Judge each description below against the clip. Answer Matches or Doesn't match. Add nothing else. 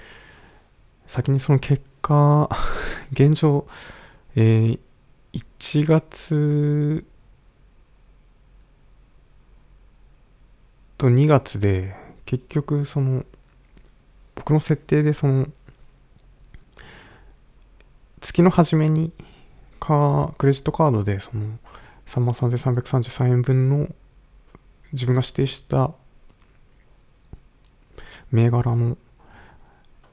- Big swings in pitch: Doesn't match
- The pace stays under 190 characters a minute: Matches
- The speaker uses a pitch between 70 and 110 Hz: Doesn't match